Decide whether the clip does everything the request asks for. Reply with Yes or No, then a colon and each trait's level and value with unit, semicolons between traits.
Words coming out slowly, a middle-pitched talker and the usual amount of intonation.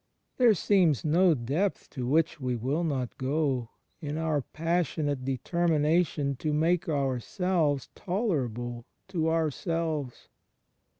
Yes: slow, 115 wpm; medium, 155 Hz; average, 4.0 semitones